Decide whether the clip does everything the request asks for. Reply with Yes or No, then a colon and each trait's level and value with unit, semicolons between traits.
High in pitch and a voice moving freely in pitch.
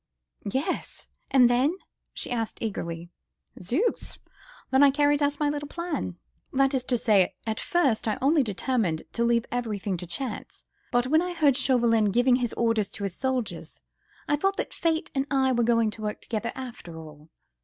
No: high, 245 Hz; average, 4.7 semitones